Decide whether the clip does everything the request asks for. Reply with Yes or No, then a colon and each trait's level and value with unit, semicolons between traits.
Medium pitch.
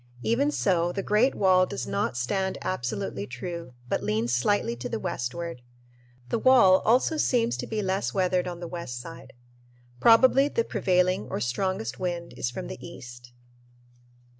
Yes: medium, 180 Hz